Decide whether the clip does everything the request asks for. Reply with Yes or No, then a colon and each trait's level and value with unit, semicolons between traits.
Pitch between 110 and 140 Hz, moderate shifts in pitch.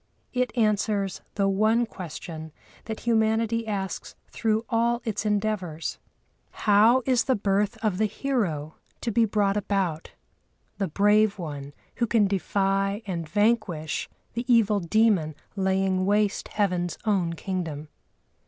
No: high, 205 Hz; average, 3.0 semitones